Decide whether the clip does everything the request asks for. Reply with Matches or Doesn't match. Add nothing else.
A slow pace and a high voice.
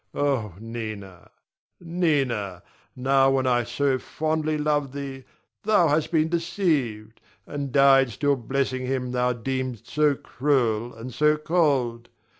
Doesn't match